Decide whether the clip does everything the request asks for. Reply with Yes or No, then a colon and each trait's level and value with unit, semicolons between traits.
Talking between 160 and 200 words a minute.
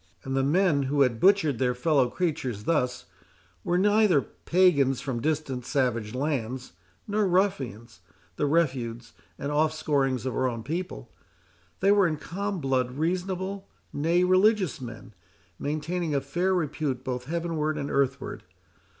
No: slow, 135 wpm